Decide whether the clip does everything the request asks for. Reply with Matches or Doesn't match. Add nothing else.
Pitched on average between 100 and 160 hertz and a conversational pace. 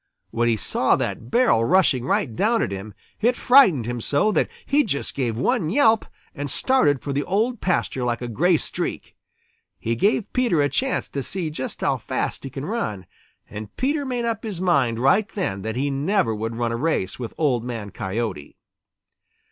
Matches